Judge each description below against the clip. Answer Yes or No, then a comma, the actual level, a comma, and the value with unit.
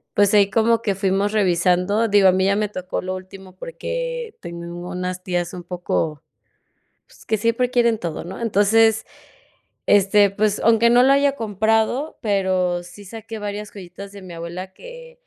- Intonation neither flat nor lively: Yes, average, 3.6 semitones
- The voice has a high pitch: Yes, high, 200 Hz